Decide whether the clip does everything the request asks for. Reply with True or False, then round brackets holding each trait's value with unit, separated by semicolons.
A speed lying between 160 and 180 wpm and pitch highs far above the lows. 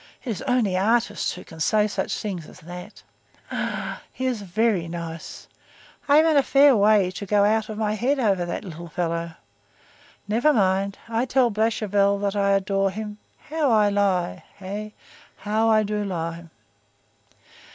False (165 wpm; 3.1 semitones)